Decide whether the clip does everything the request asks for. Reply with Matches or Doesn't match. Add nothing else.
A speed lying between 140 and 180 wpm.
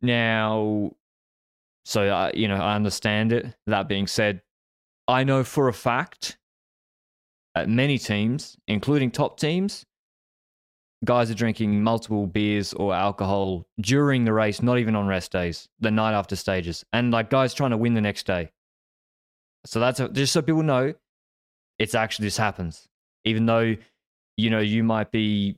Matches